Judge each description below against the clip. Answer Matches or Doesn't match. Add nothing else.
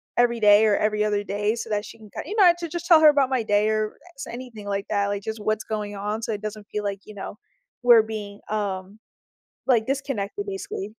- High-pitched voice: Matches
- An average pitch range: Doesn't match